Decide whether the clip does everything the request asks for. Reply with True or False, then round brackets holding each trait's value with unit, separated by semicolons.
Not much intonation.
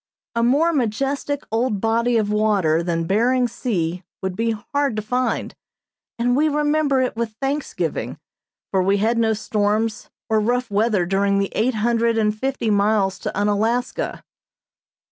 False (3.3 semitones)